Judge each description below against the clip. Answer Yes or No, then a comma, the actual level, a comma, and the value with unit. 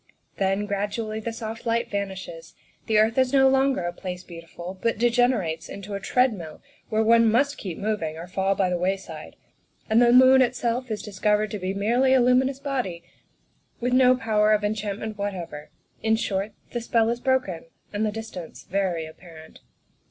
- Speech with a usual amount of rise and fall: Yes, average, 3.9 semitones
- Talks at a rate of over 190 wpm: No, average, 175 wpm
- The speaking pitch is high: Yes, high, 215 Hz